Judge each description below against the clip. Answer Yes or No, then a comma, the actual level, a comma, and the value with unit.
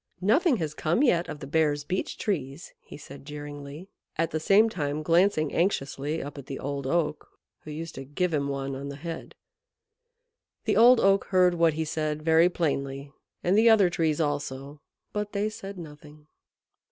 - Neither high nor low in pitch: Yes, medium, 155 Hz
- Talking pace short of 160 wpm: No, average, 175 wpm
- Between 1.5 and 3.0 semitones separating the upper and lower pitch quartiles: No, average, 4.0 semitones